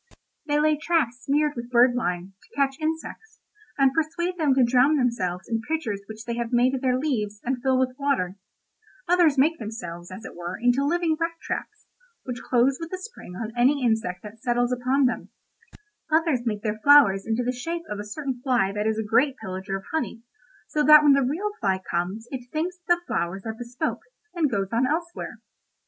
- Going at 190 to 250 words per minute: Yes, average, 200 wpm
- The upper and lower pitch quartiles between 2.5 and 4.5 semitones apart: No, average, 5.3 semitones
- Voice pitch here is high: Yes, very high, 250 Hz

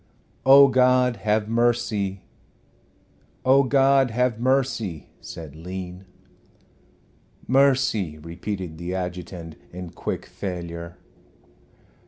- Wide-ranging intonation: Yes, wide, 6.4 semitones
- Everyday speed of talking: No, slow, 95 wpm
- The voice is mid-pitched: No, low, 100 Hz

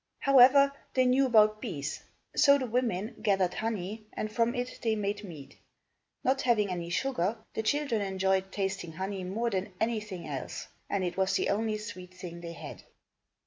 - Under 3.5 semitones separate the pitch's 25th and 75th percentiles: No, average, 4.1 semitones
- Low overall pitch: No, high, 210 Hz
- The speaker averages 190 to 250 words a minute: No, average, 170 wpm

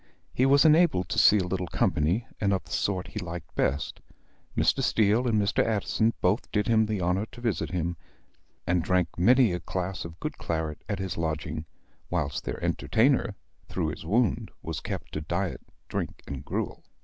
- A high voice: No, very low, 95 Hz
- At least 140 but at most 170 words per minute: No, average, 185 wpm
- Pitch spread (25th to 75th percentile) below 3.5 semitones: No, average, 4.6 semitones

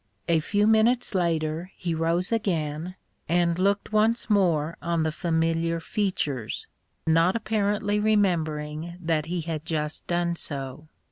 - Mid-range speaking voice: Yes, medium, 170 Hz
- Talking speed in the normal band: No, slow, 130 wpm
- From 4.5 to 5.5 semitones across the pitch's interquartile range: No, average, 4.0 semitones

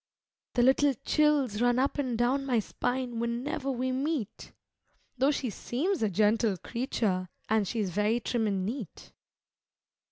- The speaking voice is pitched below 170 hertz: No, high, 240 Hz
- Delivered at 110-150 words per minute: Yes, average, 140 wpm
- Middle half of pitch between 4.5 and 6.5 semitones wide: No, average, 3.7 semitones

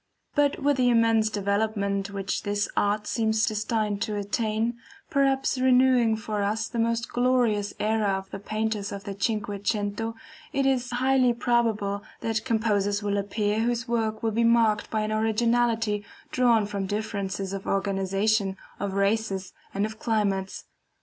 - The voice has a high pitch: Yes, high, 215 Hz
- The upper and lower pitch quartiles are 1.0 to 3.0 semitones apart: Yes, narrow, 2.4 semitones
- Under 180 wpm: Yes, average, 150 wpm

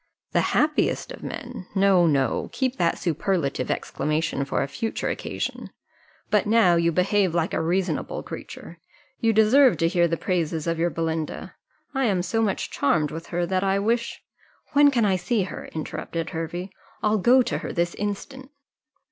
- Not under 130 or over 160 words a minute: No, average, 175 wpm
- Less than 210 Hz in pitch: Yes, medium, 185 Hz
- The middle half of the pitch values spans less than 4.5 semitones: No, average, 5.0 semitones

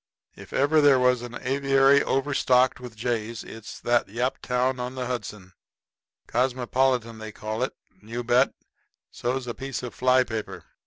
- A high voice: No, low, 125 Hz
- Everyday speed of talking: Yes, average, 155 wpm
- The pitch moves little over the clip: Yes, narrow, 1.9 semitones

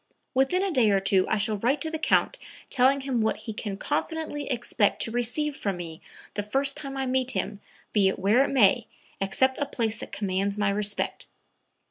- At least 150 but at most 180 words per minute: No, average, 200 wpm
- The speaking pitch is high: Yes, high, 235 Hz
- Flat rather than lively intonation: No, average, 5.1 semitones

